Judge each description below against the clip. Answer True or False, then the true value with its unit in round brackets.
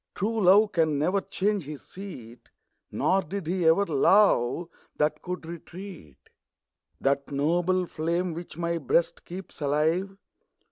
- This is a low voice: False (170 Hz)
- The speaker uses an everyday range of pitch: True (3.9 semitones)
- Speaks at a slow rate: True (130 wpm)